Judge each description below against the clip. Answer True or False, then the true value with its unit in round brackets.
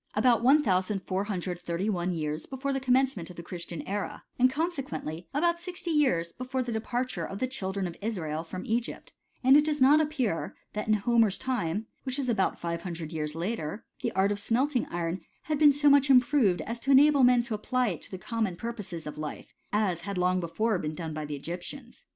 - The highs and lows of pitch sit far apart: True (6.9 semitones)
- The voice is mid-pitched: False (215 Hz)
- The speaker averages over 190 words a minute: True (200 wpm)